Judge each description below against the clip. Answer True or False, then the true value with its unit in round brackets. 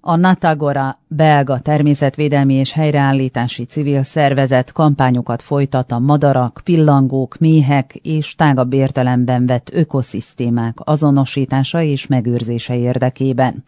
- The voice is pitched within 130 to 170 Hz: True (135 Hz)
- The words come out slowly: True (100 wpm)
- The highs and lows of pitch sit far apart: False (2.8 semitones)